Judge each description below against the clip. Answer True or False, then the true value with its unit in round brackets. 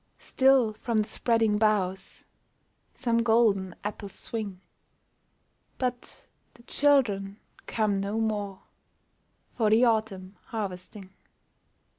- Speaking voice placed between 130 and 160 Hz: False (215 Hz)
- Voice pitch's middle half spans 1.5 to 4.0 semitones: True (2.8 semitones)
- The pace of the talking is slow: True (95 wpm)